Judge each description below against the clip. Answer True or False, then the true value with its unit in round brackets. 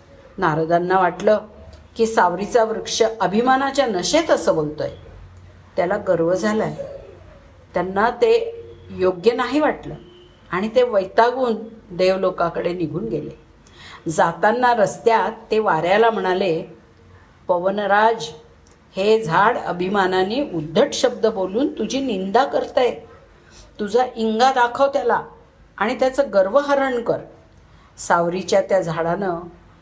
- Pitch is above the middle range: True (200 Hz)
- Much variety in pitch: True (5.8 semitones)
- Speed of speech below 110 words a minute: True (100 wpm)